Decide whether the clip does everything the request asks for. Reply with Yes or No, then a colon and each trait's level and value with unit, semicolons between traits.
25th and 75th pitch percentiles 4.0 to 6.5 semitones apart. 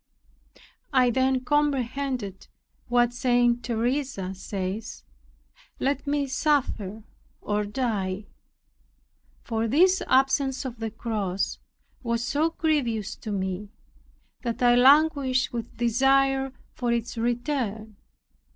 No: average, 3.5 semitones